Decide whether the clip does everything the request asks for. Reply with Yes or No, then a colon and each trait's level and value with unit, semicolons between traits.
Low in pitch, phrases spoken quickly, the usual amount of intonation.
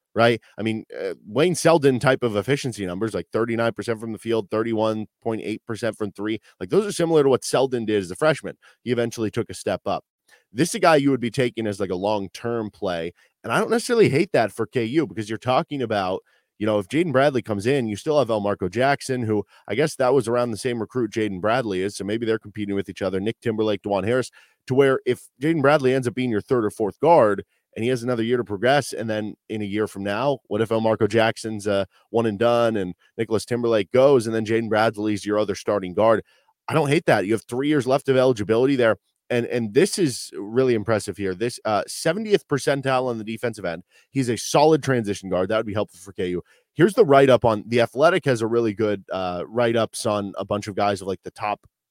Yes: low, 115 Hz; fast, 235 wpm; average, 3.4 semitones